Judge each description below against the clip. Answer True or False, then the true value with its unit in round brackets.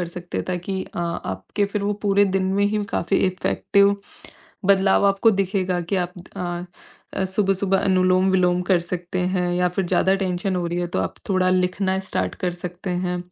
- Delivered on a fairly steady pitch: True (1.6 semitones)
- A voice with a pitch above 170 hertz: True (185 Hz)